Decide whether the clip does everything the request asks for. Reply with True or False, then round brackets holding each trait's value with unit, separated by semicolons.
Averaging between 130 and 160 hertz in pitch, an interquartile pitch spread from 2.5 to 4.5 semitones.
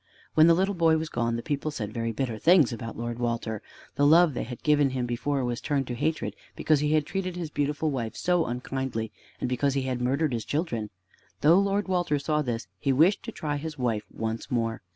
False (140 Hz; 5.0 semitones)